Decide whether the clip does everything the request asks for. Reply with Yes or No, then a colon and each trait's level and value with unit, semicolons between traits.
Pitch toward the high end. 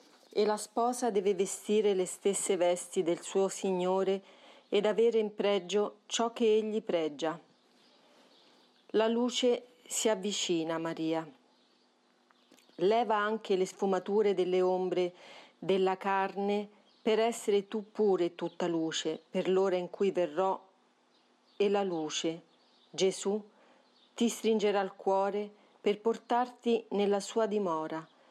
Yes: high, 200 Hz